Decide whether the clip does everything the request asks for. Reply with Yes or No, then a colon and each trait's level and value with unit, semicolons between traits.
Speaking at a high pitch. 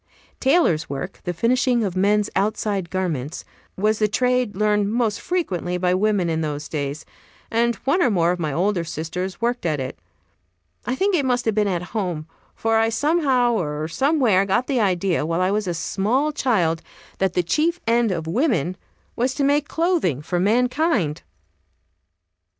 Yes: high, 205 Hz